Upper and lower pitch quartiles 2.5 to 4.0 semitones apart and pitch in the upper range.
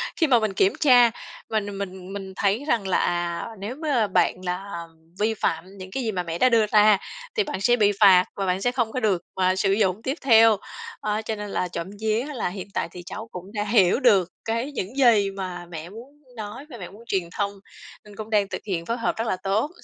Yes: average, 3.4 semitones; high, 205 Hz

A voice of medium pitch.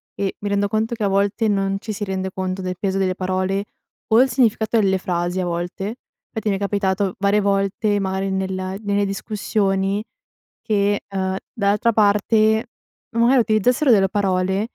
No: high, 200 Hz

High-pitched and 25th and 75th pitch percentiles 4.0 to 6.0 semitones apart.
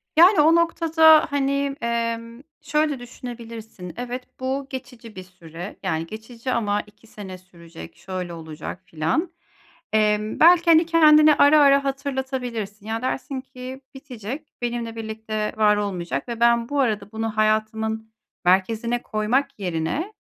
Yes: high, 230 Hz; average, 4.7 semitones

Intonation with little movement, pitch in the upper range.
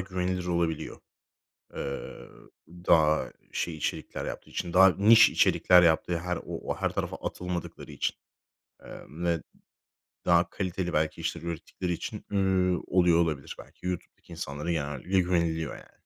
No: narrow, 2.0 semitones; very low, 85 Hz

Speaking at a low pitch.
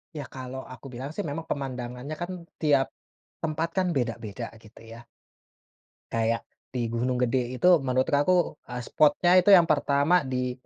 Yes: low, 130 Hz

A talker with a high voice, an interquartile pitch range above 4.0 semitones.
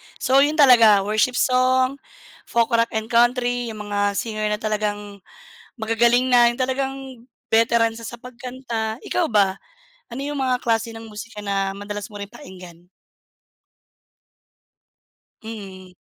No: high, 225 Hz; average, 3.2 semitones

